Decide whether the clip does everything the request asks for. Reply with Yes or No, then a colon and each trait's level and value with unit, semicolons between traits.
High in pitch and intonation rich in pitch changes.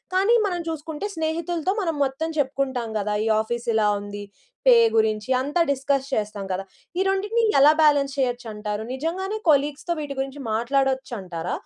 Yes: very high, 275 Hz; wide, 6.3 semitones